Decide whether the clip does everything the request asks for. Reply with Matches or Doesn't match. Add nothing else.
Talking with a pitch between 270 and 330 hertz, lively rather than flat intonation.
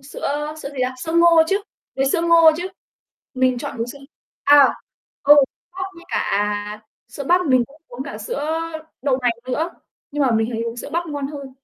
Doesn't match